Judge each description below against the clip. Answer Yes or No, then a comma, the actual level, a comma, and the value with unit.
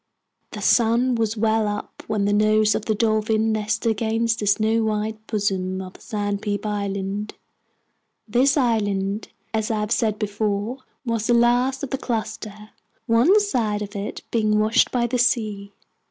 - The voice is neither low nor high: No, high, 215 Hz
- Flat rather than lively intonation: Yes, narrow, 1.9 semitones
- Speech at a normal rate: Yes, average, 155 wpm